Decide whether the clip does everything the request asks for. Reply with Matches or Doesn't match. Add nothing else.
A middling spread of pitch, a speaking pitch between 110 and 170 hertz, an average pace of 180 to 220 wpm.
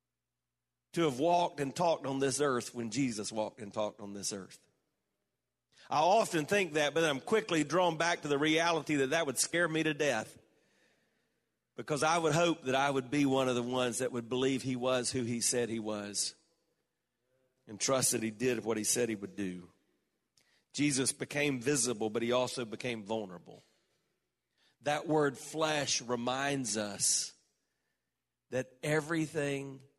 Doesn't match